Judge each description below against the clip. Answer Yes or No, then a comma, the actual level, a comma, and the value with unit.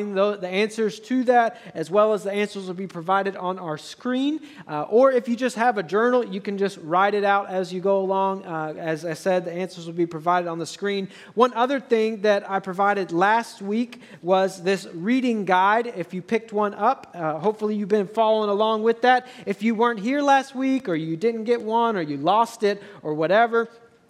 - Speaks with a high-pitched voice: Yes, high, 205 Hz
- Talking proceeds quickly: Yes, fast, 215 wpm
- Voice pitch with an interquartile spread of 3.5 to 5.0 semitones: Yes, average, 4.0 semitones